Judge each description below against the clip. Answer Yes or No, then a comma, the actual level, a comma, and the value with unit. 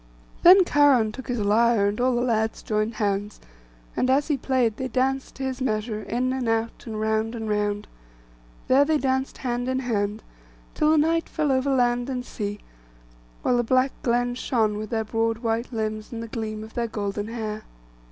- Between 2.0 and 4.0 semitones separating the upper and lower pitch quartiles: Yes, average, 3.2 semitones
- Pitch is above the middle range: Yes, high, 235 Hz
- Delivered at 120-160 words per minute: No, average, 190 wpm